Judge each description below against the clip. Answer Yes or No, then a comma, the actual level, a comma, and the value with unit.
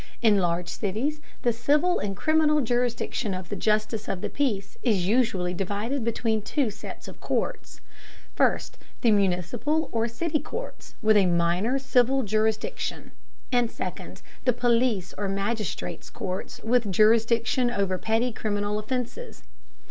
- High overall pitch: Yes, high, 225 Hz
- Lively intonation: No, average, 3.7 semitones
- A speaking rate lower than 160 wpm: Yes, average, 140 wpm